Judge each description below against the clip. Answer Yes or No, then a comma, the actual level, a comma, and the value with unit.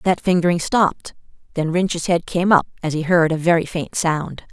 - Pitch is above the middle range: No, medium, 170 Hz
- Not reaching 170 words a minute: No, average, 200 wpm